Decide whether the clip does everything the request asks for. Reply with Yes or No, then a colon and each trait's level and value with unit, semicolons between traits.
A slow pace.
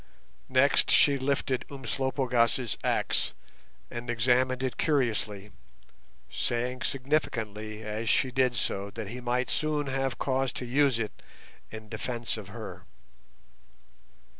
Yes: slow, 115 wpm